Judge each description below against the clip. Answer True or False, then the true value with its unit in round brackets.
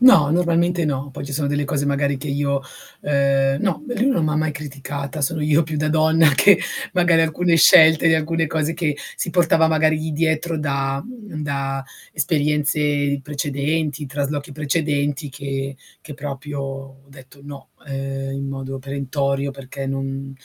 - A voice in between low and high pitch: True (145 Hz)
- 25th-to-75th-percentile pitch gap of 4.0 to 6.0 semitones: False (2.4 semitones)